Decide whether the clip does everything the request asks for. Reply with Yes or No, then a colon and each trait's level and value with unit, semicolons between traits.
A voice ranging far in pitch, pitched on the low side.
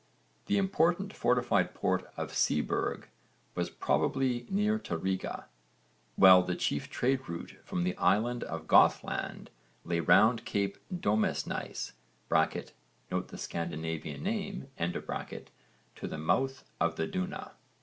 Yes: wide, 8.3 semitones; low, 110 Hz